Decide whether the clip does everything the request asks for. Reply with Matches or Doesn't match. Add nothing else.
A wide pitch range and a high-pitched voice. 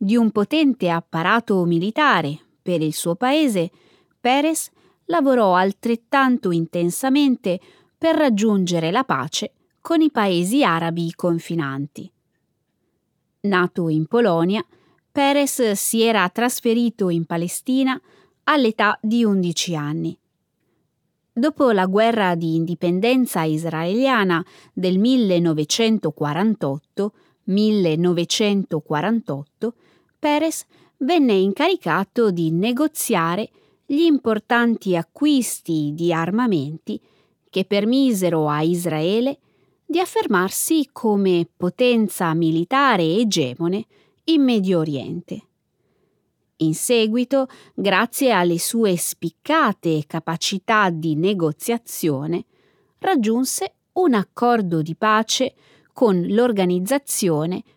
Matches